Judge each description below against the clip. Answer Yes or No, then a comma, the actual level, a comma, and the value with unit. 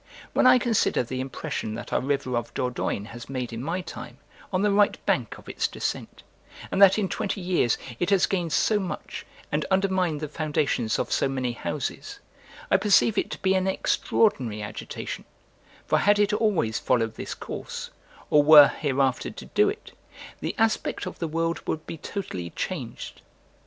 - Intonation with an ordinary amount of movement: No, wide, 7.5 semitones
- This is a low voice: No, medium, 160 Hz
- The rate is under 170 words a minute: No, average, 175 wpm